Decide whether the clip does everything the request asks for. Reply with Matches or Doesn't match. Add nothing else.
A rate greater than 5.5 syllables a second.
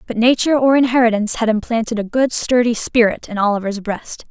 Matches